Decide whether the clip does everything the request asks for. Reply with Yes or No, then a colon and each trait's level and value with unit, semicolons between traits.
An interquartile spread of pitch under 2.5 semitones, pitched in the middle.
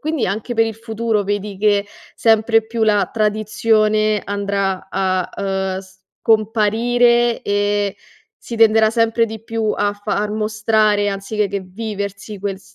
No: narrow, 1.8 semitones; high, 215 Hz